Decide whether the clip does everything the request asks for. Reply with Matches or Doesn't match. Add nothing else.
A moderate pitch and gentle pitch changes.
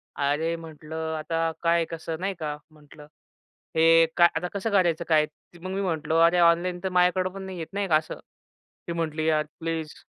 Matches